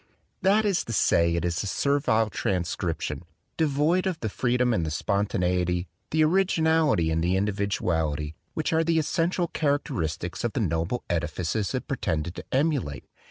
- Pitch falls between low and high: No, low, 105 Hz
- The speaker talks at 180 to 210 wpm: No, average, 160 wpm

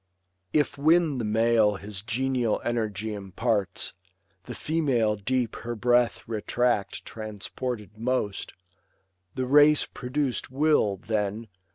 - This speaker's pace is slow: Yes, slow, 105 wpm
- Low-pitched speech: Yes, low, 115 Hz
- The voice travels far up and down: No, average, 3.4 semitones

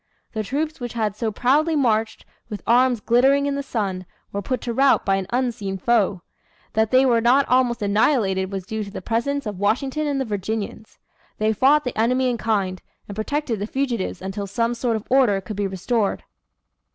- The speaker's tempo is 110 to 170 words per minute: No, average, 195 wpm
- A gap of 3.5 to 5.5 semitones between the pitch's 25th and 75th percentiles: Yes, average, 4.1 semitones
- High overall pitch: Yes, high, 230 Hz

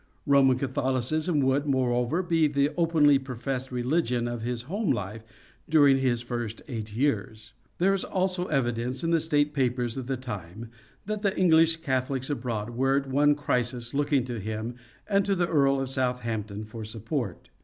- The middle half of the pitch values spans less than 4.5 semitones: Yes, average, 3.8 semitones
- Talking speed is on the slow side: No, average, 165 wpm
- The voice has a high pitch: No, low, 130 Hz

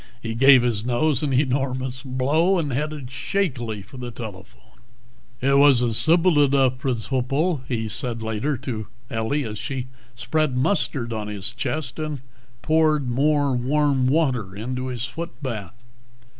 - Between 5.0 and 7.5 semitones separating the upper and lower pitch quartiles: No, average, 3.6 semitones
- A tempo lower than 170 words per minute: Yes, average, 145 wpm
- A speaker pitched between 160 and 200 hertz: No, low, 130 Hz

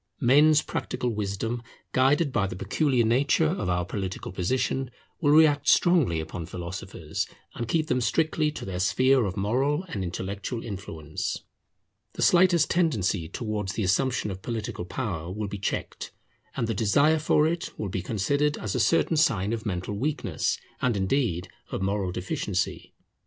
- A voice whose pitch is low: Yes, low, 110 Hz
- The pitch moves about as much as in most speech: No, wide, 7.2 semitones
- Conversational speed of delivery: Yes, average, 155 wpm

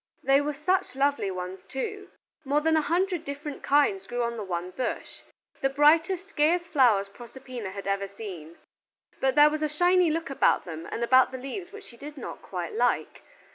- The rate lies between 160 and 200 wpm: Yes, average, 190 wpm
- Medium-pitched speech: No, very high, 275 Hz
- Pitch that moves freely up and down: Yes, wide, 6.7 semitones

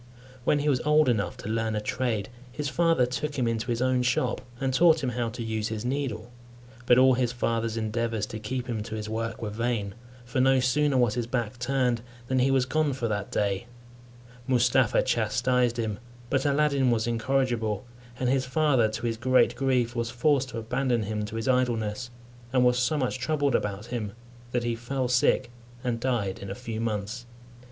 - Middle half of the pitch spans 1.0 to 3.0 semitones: Yes, narrow, 2.5 semitones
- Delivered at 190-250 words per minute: Yes, average, 195 wpm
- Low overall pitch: Yes, low, 120 Hz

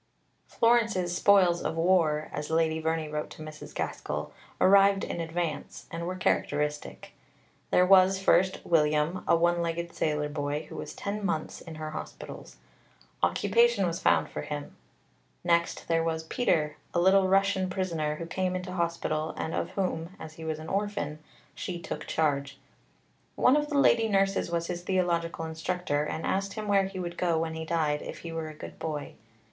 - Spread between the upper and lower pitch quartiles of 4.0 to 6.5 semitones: No, average, 3.2 semitones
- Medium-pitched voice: Yes, medium, 170 Hz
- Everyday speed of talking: Yes, average, 175 wpm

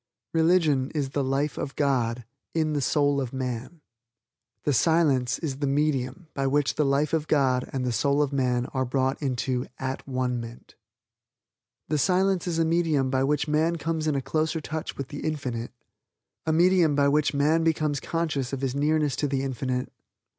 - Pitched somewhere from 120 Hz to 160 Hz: Yes, medium, 140 Hz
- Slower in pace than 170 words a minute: No, average, 180 wpm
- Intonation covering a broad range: No, average, 3.0 semitones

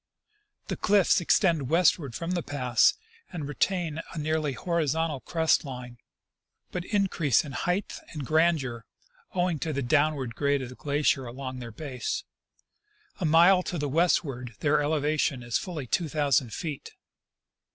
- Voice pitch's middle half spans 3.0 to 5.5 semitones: Yes, average, 4.0 semitones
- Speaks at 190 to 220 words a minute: No, average, 150 wpm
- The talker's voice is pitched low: No, medium, 150 Hz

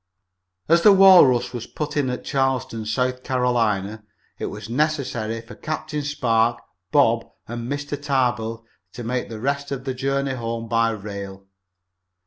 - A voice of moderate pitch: No, low, 125 Hz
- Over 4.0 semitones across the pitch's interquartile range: No, average, 3.6 semitones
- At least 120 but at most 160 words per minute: Yes, average, 150 wpm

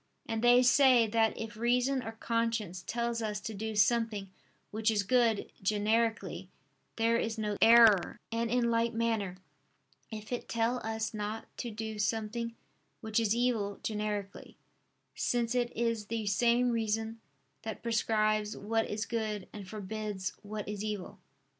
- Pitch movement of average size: No, narrow, 1.7 semitones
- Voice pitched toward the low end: No, high, 225 Hz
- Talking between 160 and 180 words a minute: No, average, 145 wpm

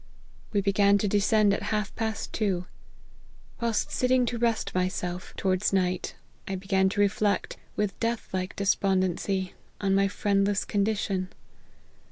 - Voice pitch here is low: No, high, 200 Hz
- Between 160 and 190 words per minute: No, average, 140 wpm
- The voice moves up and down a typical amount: No, narrow, 1.9 semitones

